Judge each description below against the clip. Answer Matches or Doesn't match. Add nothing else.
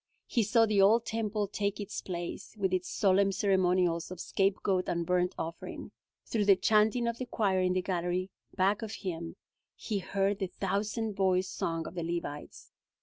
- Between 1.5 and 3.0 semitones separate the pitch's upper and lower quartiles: Matches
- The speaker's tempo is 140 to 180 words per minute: Matches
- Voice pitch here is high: Matches